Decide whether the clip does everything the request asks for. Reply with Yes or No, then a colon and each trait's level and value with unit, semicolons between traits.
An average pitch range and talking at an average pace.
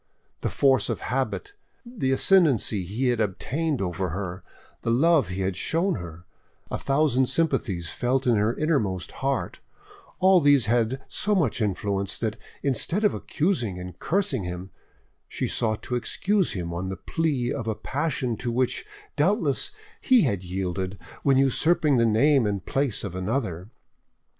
No: wide, 7.1 semitones; average, 155 wpm